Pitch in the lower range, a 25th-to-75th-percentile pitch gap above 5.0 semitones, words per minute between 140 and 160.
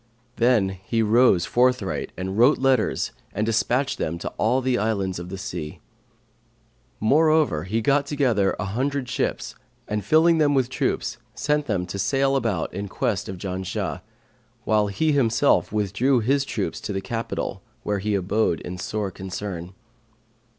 Yes: low, 110 Hz; wide, 5.5 semitones; average, 155 wpm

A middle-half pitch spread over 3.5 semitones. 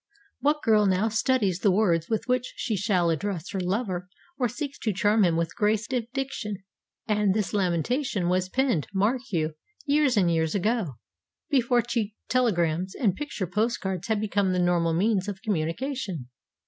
Yes: average, 4.6 semitones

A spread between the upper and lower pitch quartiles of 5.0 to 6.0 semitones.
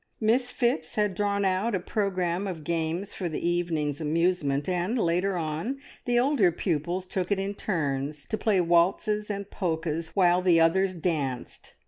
No: average, 3.5 semitones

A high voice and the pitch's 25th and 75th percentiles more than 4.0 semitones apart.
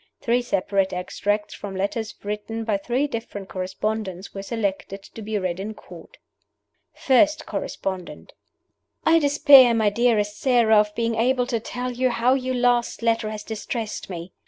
No: high, 220 Hz; average, 3.4 semitones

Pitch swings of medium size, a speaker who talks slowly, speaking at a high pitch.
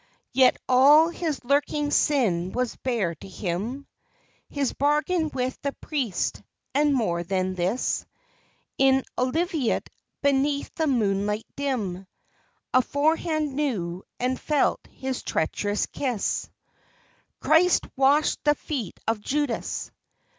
No: wide, 5.9 semitones; slow, 110 wpm; very high, 265 Hz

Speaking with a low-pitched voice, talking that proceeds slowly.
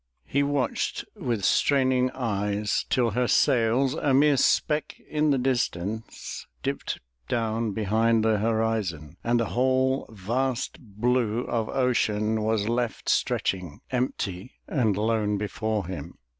Yes: low, 115 Hz; slow, 125 wpm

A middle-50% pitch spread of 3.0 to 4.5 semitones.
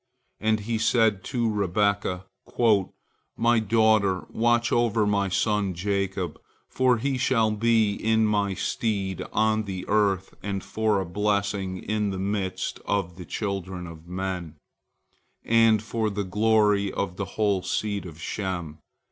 No: narrow, 2.5 semitones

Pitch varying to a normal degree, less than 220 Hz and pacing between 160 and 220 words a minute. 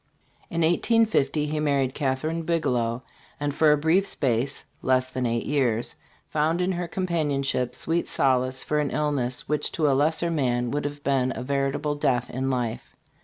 Yes: average, 3.4 semitones; medium, 140 Hz; average, 170 wpm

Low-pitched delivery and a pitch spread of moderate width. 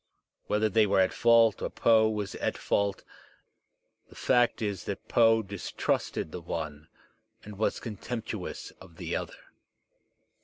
Yes: low, 105 Hz; average, 3.0 semitones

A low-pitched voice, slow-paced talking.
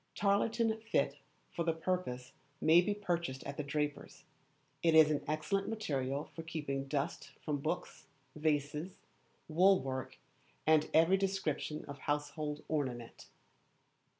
No: medium, 155 Hz; slow, 125 wpm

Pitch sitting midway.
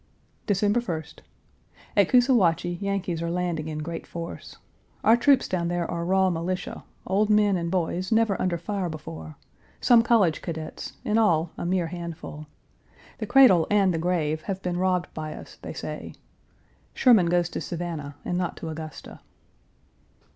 Yes: medium, 175 Hz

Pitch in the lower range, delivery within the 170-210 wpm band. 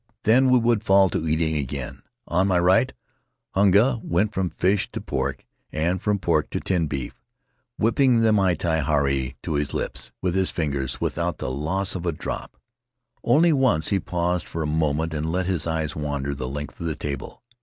Yes: very low, 85 Hz; average, 185 wpm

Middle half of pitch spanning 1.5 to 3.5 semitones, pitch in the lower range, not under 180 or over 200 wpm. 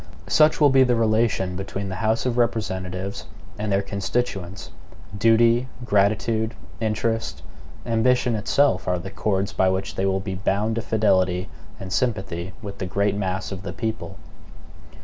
No: average, 3.2 semitones; low, 100 Hz; average, 150 wpm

